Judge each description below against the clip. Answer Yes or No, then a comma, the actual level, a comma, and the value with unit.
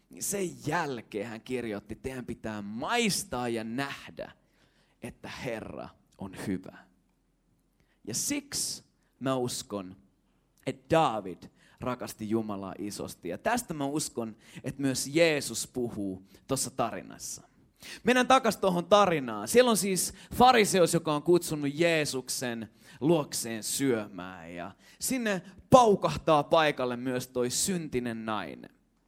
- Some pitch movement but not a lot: No, wide, 7.4 semitones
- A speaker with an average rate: Yes, average, 115 wpm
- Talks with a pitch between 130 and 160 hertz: Yes, low, 135 Hz